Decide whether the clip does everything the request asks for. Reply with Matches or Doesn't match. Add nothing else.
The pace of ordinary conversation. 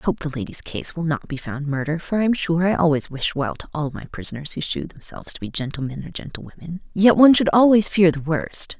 Doesn't match